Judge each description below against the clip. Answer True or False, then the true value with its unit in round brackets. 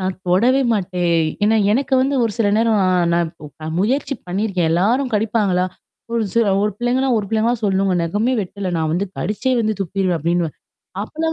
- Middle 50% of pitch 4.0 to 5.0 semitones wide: True (4.3 semitones)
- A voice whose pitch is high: True (205 Hz)